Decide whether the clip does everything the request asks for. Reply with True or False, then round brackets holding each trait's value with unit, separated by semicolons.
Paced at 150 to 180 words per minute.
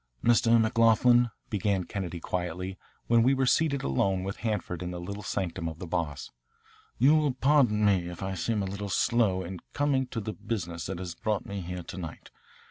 False (195 wpm)